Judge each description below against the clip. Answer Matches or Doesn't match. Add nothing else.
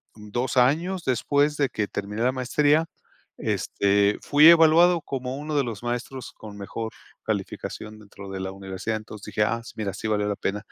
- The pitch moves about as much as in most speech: Doesn't match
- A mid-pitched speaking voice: Doesn't match